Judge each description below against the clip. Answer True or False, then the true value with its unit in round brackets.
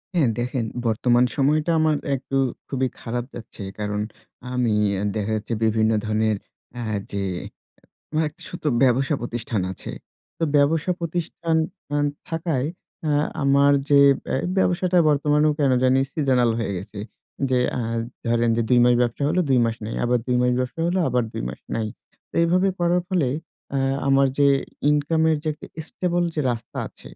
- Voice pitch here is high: False (135 Hz)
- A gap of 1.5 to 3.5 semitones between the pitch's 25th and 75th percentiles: False (4.8 semitones)